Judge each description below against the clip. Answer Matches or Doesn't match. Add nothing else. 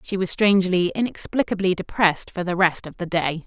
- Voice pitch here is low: Doesn't match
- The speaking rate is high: Doesn't match